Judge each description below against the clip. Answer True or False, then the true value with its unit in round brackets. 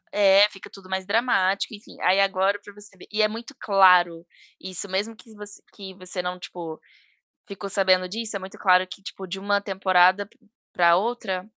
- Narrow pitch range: True (1.8 semitones)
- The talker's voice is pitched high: True (195 Hz)